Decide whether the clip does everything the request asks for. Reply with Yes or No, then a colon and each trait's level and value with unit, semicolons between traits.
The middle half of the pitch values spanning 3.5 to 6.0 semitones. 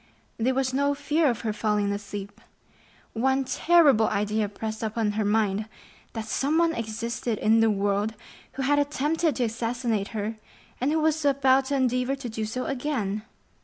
Yes: average, 4.2 semitones